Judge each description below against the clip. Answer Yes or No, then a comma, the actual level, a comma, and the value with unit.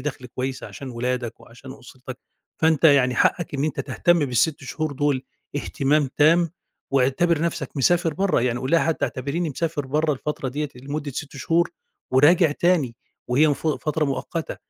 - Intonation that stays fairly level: No, average, 3.6 semitones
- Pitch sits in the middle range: Yes, medium, 145 Hz